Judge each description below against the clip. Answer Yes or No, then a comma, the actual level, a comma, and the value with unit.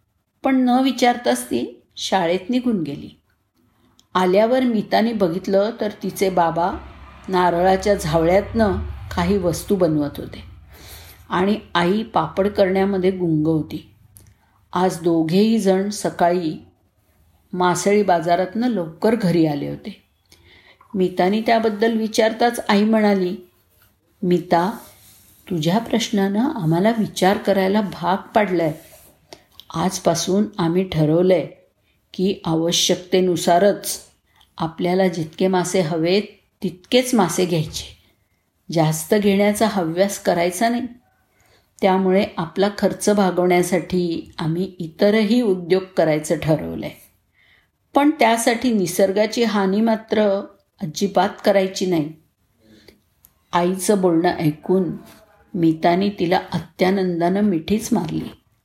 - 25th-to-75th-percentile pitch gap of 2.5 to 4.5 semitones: Yes, average, 3.9 semitones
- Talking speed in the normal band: Yes, average, 95 wpm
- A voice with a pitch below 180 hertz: No, medium, 185 Hz